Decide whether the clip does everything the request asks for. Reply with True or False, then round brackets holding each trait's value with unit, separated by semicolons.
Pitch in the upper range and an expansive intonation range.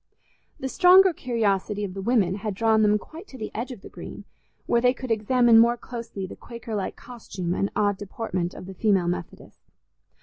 False (220 Hz; 3.6 semitones)